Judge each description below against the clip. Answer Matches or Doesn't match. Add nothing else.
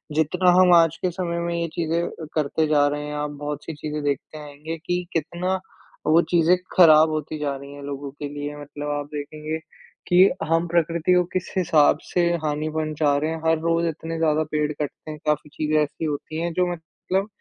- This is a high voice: Doesn't match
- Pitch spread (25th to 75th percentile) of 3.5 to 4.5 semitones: Doesn't match